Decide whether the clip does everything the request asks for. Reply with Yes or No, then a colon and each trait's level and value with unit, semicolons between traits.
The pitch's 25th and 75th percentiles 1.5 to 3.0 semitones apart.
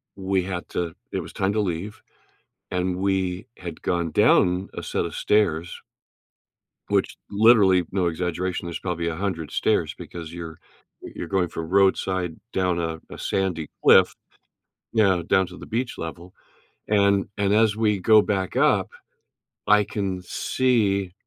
Yes: narrow, 2.6 semitones